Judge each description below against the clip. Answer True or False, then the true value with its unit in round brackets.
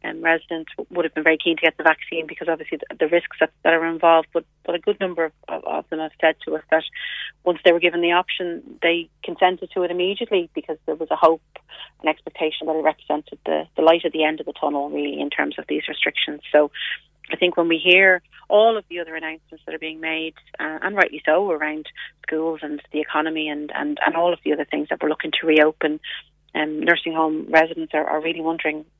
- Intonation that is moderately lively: False (1.8 semitones)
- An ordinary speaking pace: False (240 wpm)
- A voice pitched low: False (160 Hz)